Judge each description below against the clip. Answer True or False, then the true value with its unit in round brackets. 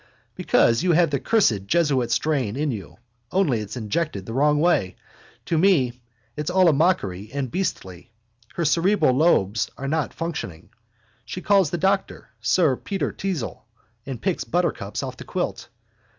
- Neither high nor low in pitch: True (150 Hz)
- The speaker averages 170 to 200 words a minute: False (155 wpm)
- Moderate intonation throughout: False (6.9 semitones)